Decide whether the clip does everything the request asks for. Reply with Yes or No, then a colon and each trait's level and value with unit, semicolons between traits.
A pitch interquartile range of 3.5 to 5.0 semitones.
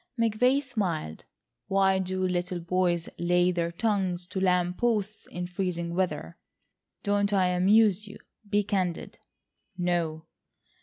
No: narrow, 2.5 semitones